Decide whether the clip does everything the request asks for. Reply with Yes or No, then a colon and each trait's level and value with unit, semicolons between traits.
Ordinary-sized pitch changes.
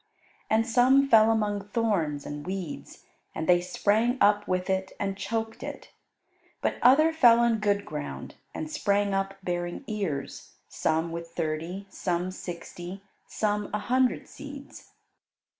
Yes: average, 4.3 semitones